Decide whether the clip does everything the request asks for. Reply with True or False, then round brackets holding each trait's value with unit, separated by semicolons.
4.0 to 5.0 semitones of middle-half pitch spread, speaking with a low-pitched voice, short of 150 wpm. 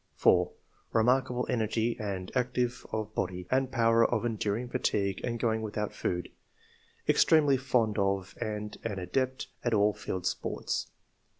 False (3.2 semitones; 115 Hz; 140 wpm)